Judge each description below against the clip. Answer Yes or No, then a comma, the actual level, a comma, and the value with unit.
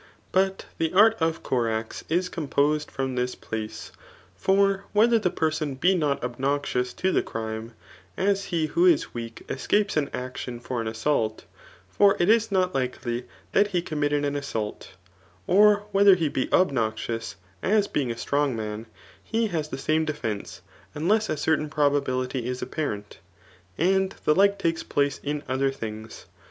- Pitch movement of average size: No, wide, 7.2 semitones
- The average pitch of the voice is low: No, medium, 145 Hz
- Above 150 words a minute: Yes, average, 160 wpm